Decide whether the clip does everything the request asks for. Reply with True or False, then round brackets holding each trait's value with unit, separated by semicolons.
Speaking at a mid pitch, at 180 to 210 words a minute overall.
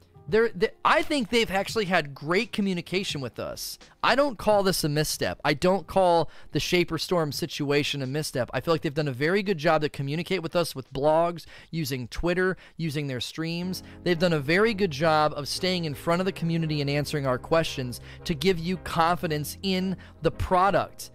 True (165 Hz; 200 wpm)